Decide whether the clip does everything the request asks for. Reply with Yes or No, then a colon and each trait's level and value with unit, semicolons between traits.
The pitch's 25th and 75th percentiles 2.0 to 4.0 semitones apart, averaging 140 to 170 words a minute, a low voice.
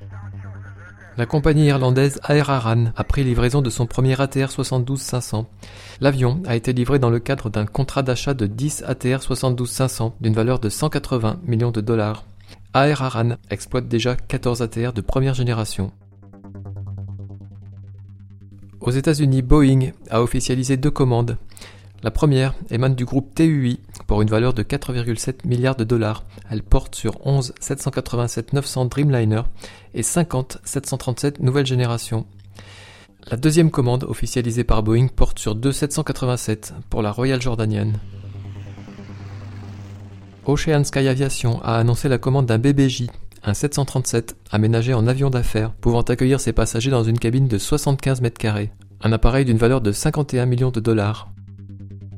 No: average, 4.4 semitones; slow, 145 wpm; low, 120 Hz